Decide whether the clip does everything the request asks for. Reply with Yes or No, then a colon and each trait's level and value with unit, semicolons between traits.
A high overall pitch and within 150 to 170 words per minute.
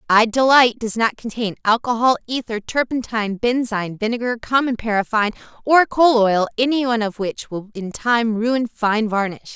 Yes: high, 230 Hz; average, 155 wpm